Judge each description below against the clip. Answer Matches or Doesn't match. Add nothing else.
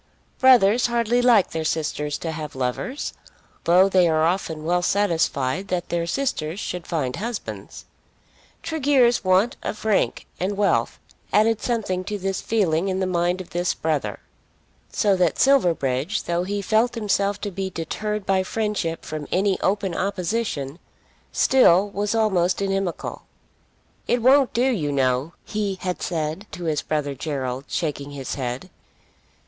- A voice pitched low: Doesn't match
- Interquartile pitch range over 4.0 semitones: Matches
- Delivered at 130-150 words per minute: Matches